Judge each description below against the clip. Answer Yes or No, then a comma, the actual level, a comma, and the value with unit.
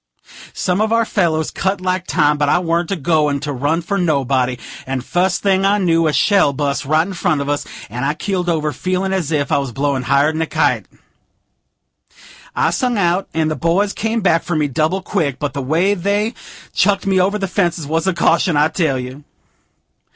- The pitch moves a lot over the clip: No, average, 4.7 semitones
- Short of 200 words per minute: No, fast, 205 wpm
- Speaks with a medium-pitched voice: Yes, medium, 165 Hz